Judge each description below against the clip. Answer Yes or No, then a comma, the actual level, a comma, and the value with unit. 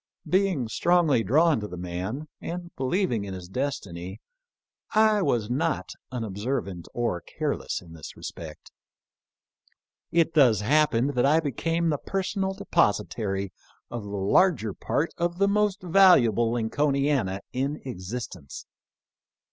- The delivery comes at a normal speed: No, slow, 130 wpm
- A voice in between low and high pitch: No, low, 130 Hz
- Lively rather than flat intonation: Yes, wide, 8.5 semitones